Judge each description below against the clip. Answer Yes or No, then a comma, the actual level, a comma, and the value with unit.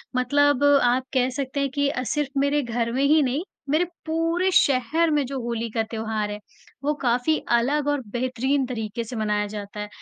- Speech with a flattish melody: No, average, 3.6 semitones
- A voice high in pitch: Yes, very high, 255 Hz